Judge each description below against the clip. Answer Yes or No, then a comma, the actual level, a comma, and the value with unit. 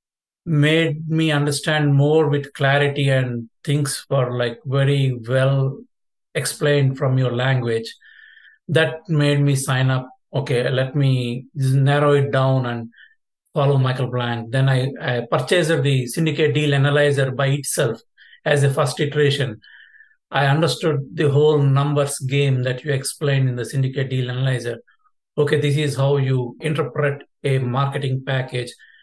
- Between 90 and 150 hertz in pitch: Yes, medium, 140 Hz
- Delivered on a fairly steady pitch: Yes, narrow, 2.1 semitones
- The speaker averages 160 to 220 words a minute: No, average, 145 wpm